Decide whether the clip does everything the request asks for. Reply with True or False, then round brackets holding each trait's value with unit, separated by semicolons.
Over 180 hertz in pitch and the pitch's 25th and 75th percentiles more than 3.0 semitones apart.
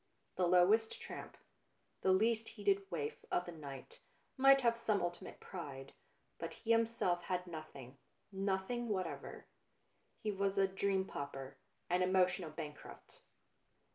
True (190 Hz; 3.7 semitones)